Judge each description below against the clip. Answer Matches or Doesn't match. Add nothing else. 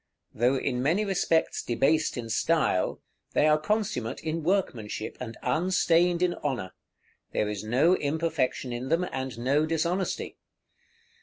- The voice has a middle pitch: Matches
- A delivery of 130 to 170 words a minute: Matches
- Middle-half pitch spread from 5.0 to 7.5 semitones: Matches